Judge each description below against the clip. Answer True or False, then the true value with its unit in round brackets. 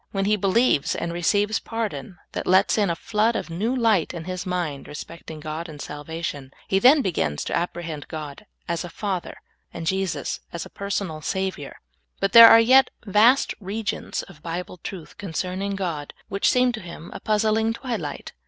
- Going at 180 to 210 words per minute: True (185 wpm)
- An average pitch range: True (4.4 semitones)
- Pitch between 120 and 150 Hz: False (185 Hz)